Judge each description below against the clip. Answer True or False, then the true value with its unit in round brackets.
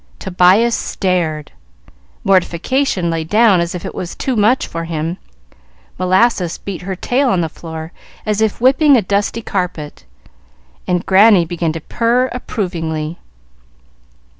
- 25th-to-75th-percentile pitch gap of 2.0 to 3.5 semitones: False (4.8 semitones)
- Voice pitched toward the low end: False (185 Hz)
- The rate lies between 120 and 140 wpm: True (135 wpm)